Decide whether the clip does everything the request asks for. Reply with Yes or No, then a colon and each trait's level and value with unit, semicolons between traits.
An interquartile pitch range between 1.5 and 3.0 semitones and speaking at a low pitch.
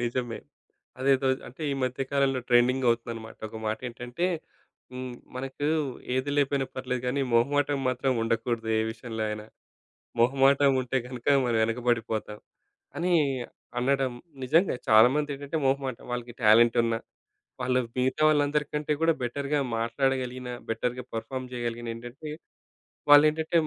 Yes: average, 2.7 semitones; low, 125 Hz